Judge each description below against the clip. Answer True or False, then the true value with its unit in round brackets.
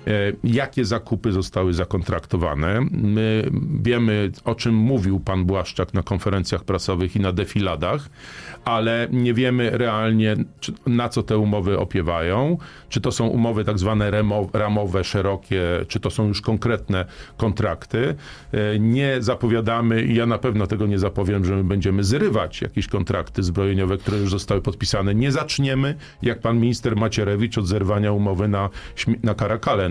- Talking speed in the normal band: True (140 wpm)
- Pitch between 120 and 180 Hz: False (105 Hz)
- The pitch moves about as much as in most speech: True (3.0 semitones)